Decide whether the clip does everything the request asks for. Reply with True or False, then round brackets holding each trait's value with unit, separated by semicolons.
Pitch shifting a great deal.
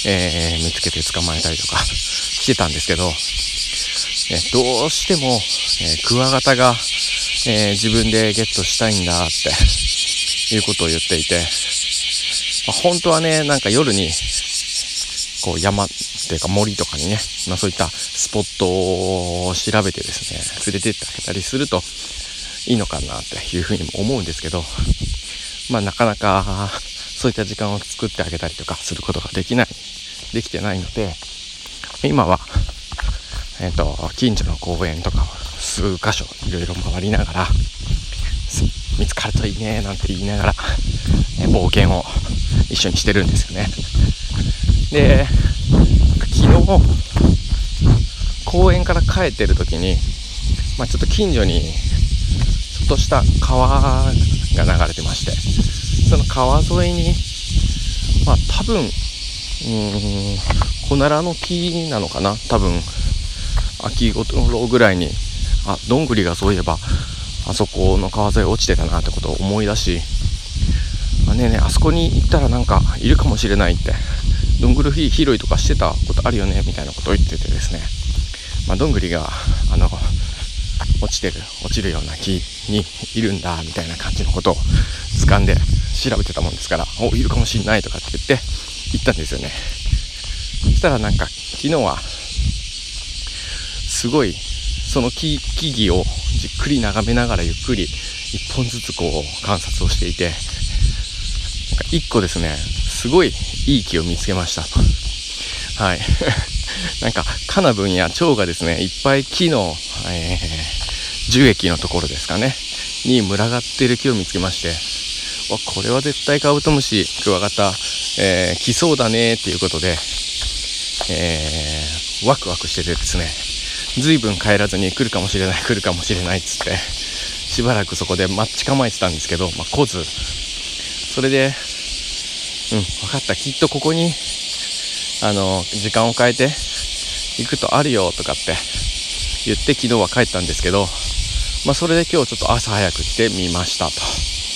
False (4.4 semitones)